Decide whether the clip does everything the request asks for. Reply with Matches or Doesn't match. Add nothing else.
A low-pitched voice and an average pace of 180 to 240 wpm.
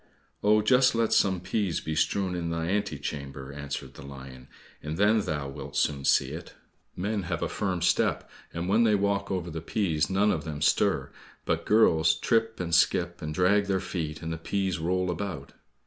Matches